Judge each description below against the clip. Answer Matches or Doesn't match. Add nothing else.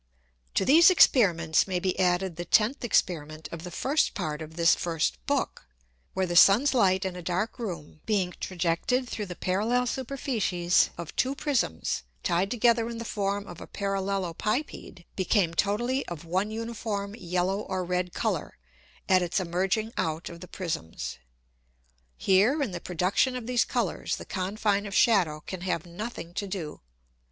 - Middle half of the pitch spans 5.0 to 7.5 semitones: Doesn't match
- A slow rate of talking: Doesn't match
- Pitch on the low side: Doesn't match